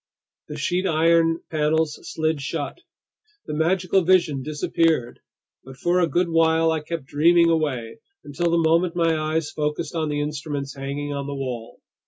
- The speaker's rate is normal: Yes, average, 160 wpm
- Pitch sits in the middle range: Yes, medium, 160 Hz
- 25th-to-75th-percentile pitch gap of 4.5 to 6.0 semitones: No, narrow, 2.4 semitones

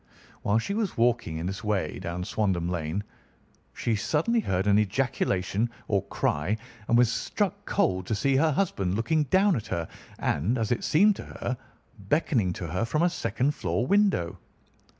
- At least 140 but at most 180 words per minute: Yes, average, 170 wpm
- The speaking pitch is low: Yes, low, 110 Hz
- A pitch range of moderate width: No, wide, 7.7 semitones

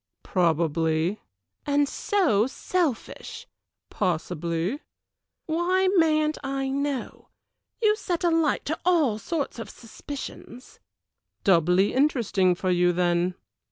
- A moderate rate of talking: No, slow, 100 wpm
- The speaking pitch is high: Yes, very high, 250 Hz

